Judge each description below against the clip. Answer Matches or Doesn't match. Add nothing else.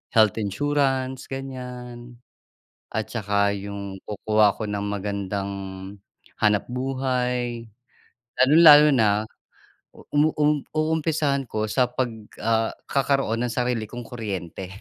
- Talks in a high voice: Doesn't match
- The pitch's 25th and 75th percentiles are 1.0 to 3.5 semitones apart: Doesn't match